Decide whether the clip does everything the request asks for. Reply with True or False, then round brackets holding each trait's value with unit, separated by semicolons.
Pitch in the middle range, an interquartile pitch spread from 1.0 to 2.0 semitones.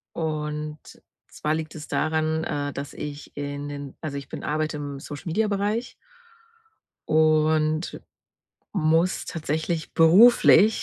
True (155 Hz; 1.7 semitones)